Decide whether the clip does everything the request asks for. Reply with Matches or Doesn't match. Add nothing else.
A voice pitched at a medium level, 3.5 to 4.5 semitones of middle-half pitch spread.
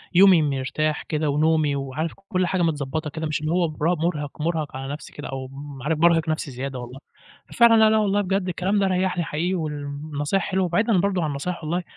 Matches